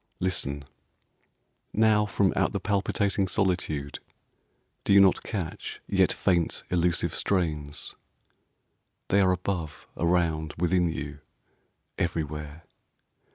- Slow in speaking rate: Yes, slow, 100 wpm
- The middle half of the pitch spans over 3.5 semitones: Yes, average, 3.9 semitones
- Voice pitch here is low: Yes, very low, 85 Hz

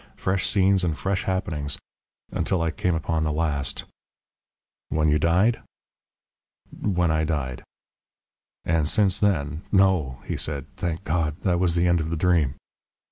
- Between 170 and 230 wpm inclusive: No, average, 155 wpm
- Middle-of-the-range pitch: No, very low, 85 Hz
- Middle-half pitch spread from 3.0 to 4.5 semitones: Yes, average, 3.4 semitones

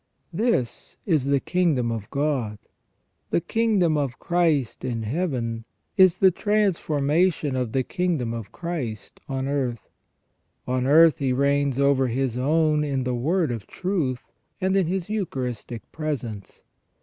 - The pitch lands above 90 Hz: Yes, medium, 140 Hz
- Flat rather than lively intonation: No, wide, 5.4 semitones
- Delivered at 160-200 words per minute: No, average, 140 wpm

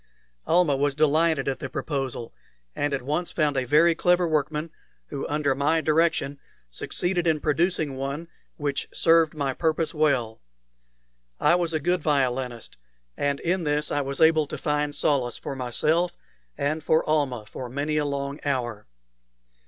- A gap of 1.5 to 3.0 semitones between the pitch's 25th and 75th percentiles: Yes, narrow, 2.6 semitones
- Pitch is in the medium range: Yes, medium, 150 Hz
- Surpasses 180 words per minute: No, average, 155 wpm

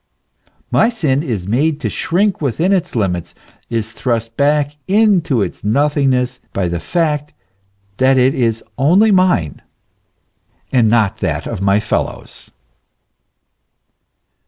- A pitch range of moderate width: No, wide, 6.2 semitones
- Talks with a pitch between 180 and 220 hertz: No, low, 135 Hz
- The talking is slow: Yes, slow, 125 wpm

